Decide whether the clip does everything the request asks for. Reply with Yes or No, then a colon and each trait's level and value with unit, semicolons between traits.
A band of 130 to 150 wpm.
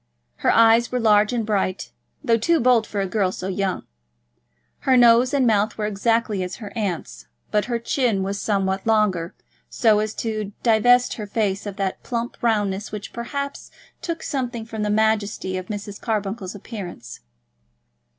No: average, 165 wpm